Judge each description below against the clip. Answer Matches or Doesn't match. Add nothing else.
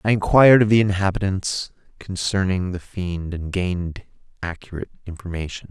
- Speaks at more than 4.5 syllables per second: Matches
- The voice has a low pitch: Matches